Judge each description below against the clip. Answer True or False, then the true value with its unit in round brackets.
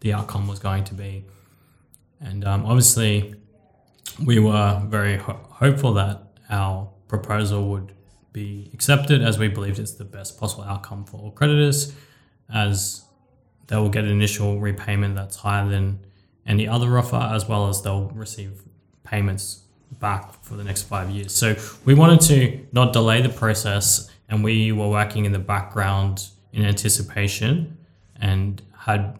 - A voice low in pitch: True (105 Hz)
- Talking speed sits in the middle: True (155 wpm)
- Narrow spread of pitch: True (2.2 semitones)